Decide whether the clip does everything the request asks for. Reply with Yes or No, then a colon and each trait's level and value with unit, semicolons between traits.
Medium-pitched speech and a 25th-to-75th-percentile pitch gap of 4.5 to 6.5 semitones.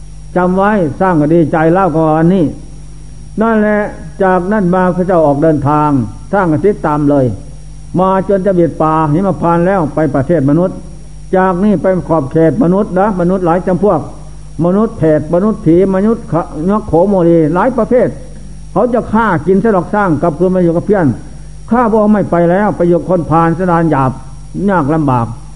No: medium, 170 Hz; average, 3.7 semitones